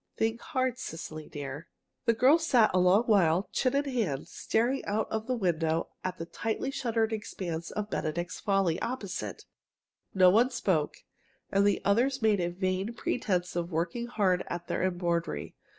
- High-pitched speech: Yes, high, 195 Hz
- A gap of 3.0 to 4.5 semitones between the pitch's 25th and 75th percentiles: No, average, 5.1 semitones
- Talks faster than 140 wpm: Yes, average, 165 wpm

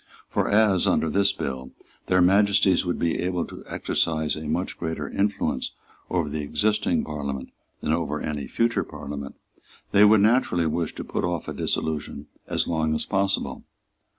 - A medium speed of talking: Yes, average, 160 wpm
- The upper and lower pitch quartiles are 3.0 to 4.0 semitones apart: No, average, 4.5 semitones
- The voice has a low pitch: Yes, very low, 85 Hz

